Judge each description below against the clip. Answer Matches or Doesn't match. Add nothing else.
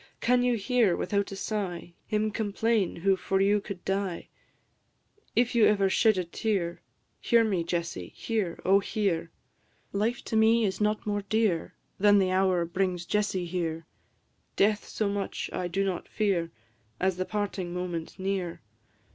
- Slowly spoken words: Doesn't match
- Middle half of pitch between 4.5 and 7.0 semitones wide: Doesn't match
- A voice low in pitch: Doesn't match